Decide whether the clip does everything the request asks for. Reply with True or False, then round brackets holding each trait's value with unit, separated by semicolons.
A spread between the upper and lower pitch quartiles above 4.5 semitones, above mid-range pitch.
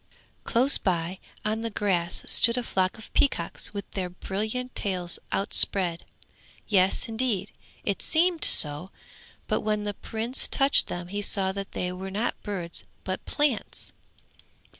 False (3.6 semitones; 200 Hz)